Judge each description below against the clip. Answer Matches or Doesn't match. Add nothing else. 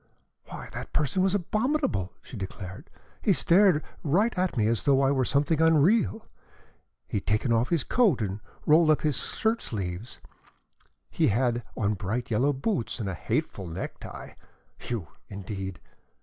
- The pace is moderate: Matches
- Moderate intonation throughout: Doesn't match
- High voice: Doesn't match